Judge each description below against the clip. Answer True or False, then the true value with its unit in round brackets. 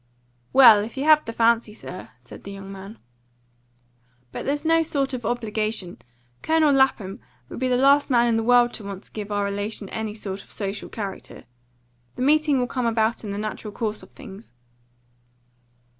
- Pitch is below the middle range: False (225 Hz)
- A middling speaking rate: True (185 wpm)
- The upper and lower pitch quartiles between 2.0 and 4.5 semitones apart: True (4.2 semitones)